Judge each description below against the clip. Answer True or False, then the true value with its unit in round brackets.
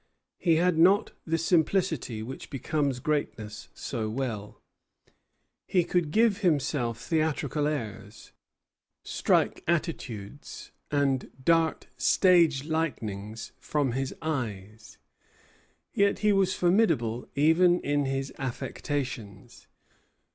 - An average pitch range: False (5.9 semitones)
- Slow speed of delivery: True (95 wpm)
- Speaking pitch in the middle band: True (145 Hz)